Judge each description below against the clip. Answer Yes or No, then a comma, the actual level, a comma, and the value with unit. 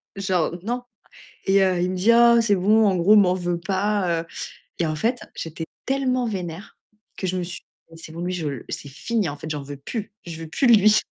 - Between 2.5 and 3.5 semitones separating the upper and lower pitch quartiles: No, average, 4.3 semitones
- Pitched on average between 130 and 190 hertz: Yes, medium, 185 Hz